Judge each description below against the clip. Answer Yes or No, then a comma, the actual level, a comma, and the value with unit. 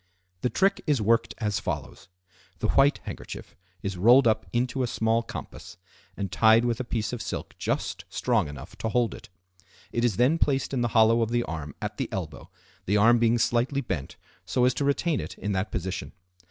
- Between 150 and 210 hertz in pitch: No, low, 115 Hz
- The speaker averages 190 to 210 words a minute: Yes, average, 195 wpm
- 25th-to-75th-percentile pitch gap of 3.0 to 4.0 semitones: Yes, average, 3.7 semitones